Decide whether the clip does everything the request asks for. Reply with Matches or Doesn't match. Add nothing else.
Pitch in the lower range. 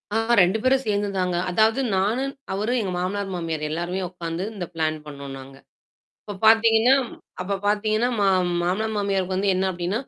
Doesn't match